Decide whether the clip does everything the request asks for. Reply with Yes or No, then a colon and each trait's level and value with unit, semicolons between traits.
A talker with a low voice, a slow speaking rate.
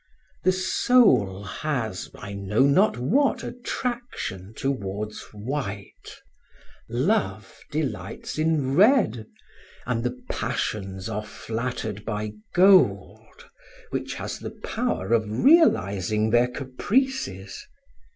Yes: low, 120 Hz; slow, 95 wpm